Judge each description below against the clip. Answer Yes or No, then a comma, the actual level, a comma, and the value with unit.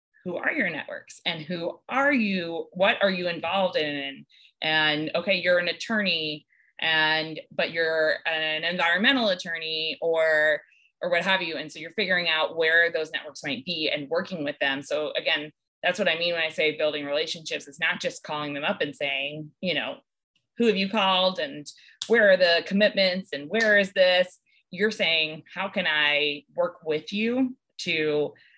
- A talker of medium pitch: Yes, medium, 170 Hz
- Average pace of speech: Yes, average, 180 wpm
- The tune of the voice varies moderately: Yes, average, 3.6 semitones